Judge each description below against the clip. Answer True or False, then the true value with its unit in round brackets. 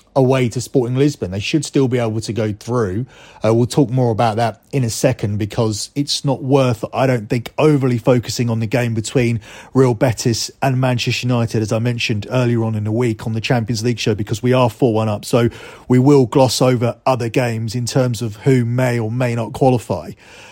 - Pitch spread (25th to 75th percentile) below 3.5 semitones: True (2.5 semitones)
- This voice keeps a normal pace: False (225 wpm)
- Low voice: True (120 Hz)